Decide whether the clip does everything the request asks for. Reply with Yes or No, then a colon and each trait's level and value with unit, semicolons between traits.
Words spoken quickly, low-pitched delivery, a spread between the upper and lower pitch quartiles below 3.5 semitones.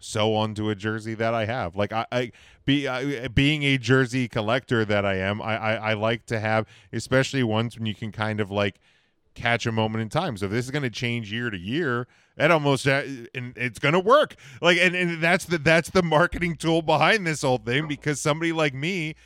No: fast, 225 wpm; low, 125 Hz; average, 4.9 semitones